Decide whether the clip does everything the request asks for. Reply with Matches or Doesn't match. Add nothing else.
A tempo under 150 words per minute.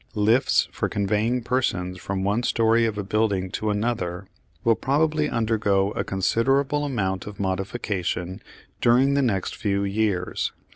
Matches